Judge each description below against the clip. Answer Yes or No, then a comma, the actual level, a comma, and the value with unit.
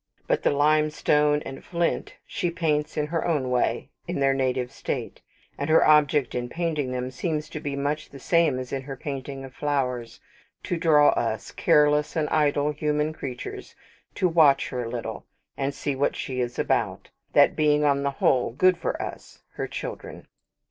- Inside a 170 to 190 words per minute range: Yes, average, 180 wpm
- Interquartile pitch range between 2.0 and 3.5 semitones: Yes, narrow, 2.5 semitones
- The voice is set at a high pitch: No, medium, 145 Hz